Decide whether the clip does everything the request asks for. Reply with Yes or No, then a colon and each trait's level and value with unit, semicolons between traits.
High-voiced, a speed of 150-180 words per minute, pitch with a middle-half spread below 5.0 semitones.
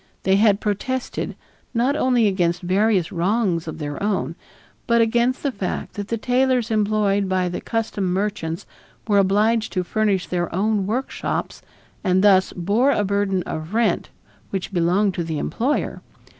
Yes: high, 200 Hz; average, 155 wpm; average, 3.6 semitones